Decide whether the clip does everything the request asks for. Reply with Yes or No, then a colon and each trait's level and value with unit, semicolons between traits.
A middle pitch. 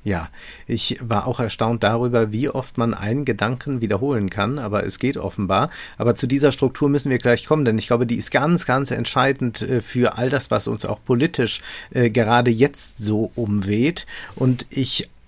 No: low, 120 Hz